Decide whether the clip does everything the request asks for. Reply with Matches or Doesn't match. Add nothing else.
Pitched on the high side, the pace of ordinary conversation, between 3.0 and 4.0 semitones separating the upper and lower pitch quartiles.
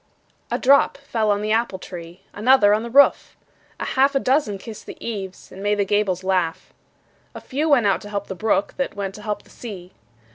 Doesn't match